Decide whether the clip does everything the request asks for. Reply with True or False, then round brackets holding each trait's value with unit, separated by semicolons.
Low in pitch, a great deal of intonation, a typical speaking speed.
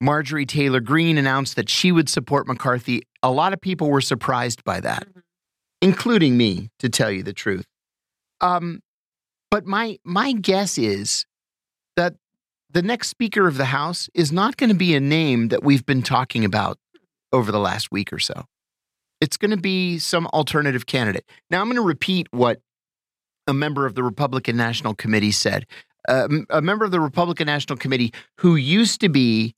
False (145 Hz; 6.4 semitones; 180 wpm)